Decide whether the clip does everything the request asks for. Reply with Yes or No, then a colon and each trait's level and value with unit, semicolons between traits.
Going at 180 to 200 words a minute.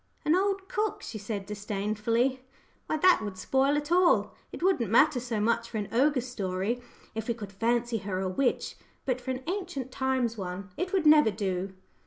Yes: average, 190 wpm